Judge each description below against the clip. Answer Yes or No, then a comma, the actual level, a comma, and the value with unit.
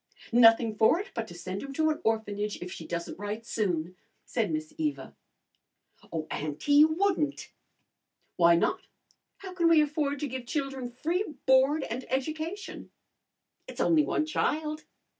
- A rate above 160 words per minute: No, average, 155 wpm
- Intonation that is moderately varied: No, wide, 6.4 semitones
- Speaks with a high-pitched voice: Yes, very high, 275 Hz